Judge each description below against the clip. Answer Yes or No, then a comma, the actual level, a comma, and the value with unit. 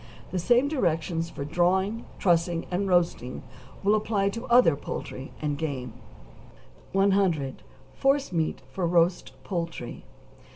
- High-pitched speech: No, medium, 175 Hz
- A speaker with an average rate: No, slow, 115 wpm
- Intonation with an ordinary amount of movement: Yes, average, 3.6 semitones